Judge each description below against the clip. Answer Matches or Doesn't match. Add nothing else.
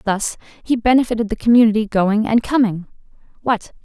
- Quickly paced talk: Doesn't match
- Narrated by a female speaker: Matches